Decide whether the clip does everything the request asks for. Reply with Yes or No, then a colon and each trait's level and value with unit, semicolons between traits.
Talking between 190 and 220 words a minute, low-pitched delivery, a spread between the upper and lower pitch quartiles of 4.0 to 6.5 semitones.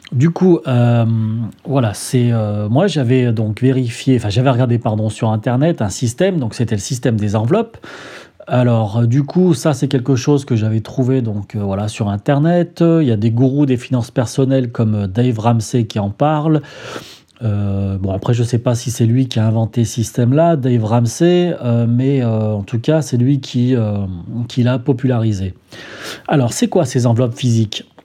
No: average, 195 wpm; low, 120 Hz; average, 3.5 semitones